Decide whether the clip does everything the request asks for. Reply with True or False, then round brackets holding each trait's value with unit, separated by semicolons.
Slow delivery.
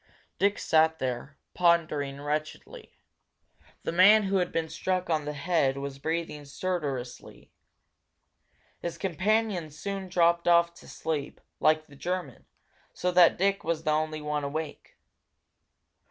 True (130 wpm)